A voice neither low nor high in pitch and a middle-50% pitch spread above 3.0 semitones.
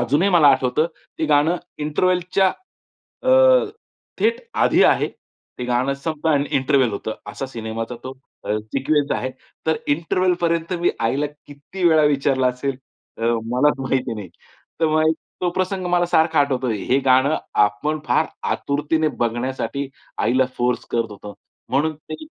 Yes: medium, 145 Hz; average, 4.0 semitones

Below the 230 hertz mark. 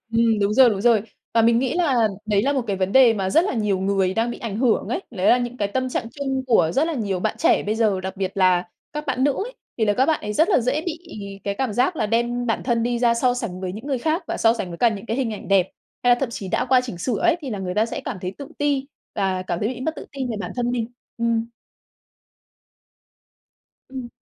No: high, 235 Hz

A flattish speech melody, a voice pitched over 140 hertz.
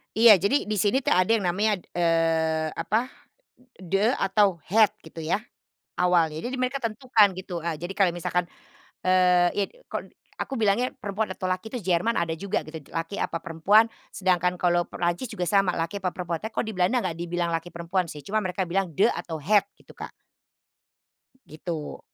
No: average, 3.7 semitones; medium, 185 Hz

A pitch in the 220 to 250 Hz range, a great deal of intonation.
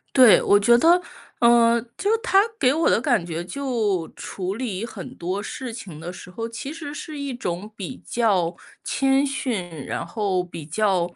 Yes: high, 225 Hz; wide, 6.4 semitones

